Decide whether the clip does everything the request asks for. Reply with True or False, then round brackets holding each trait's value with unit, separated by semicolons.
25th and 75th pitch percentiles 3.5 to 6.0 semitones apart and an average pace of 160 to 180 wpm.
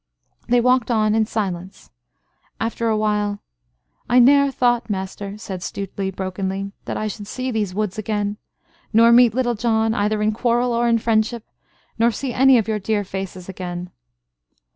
False (3.0 semitones; 165 wpm)